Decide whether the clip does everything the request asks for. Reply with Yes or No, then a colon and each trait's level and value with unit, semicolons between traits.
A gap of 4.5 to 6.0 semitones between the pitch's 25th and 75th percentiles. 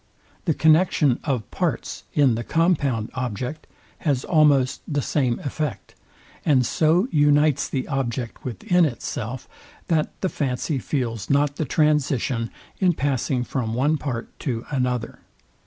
No: average, 3.7 semitones